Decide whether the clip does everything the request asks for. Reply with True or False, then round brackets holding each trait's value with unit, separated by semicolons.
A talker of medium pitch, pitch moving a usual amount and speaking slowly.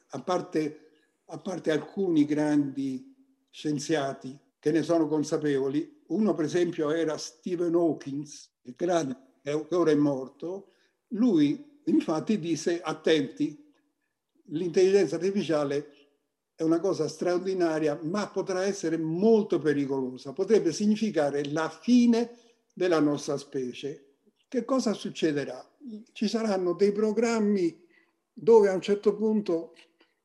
False (170 Hz; 6.5 semitones; 110 wpm)